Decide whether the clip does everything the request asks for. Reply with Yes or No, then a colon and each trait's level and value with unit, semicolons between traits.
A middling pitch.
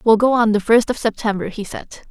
No: high, 220 Hz